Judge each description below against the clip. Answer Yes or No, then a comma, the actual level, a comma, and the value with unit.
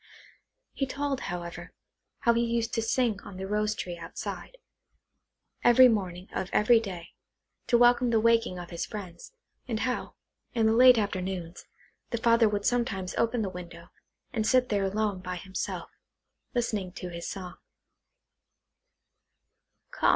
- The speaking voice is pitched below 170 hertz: No, high, 210 Hz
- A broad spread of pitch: No, average, 4.4 semitones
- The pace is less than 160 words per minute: Yes, average, 145 wpm